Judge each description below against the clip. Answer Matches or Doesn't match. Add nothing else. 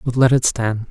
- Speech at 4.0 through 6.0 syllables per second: Matches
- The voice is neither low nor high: Doesn't match